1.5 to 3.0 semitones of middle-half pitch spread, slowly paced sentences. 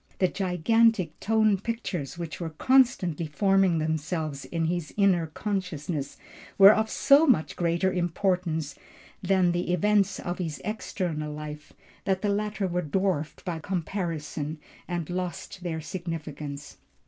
No: average, 3.7 semitones; slow, 130 wpm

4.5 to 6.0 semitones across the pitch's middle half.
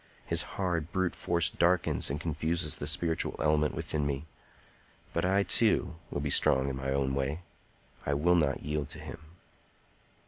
No: average, 3.3 semitones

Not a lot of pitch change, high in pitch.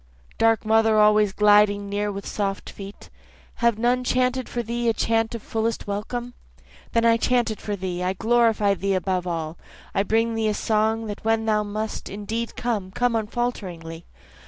Yes: narrow, 2.3 semitones; high, 215 Hz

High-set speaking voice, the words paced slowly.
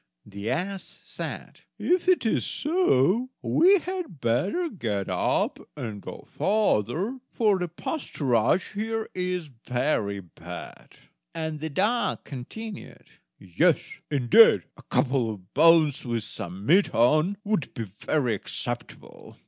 No: medium, 155 Hz; slow, 125 wpm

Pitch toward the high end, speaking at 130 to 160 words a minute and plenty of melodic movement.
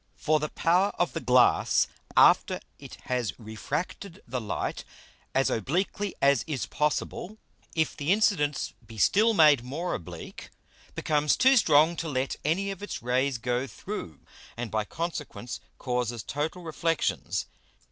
No: medium, 150 Hz; average, 140 wpm; wide, 5.7 semitones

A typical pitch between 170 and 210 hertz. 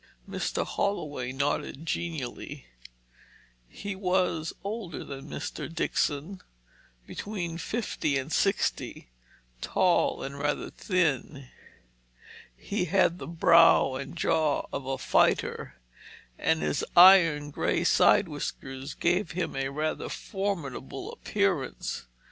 No: medium, 160 Hz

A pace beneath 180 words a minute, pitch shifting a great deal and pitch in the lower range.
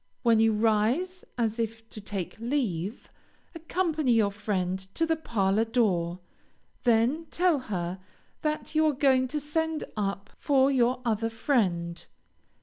No: average, 140 wpm; wide, 6.0 semitones; high, 230 Hz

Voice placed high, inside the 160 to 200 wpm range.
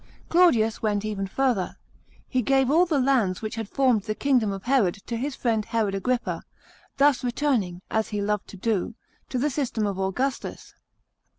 Yes: high, 230 Hz; average, 175 wpm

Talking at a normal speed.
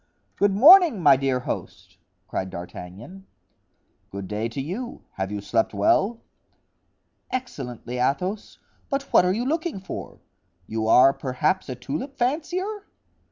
No: slow, 130 wpm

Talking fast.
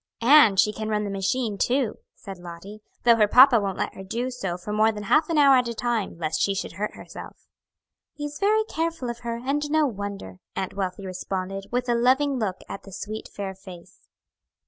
Yes: fast, 210 wpm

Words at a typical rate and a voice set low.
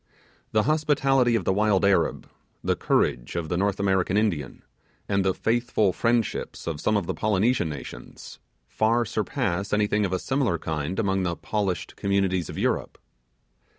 Yes: average, 155 wpm; low, 100 Hz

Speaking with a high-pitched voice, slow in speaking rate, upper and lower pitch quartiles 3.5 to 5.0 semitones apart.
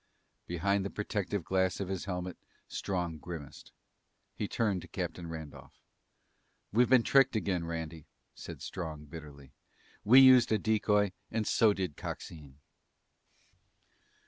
No: very low, 95 Hz; slow, 125 wpm; average, 4.2 semitones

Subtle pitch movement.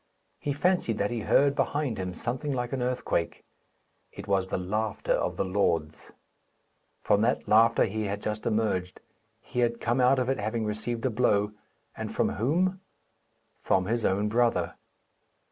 No: average, 3.5 semitones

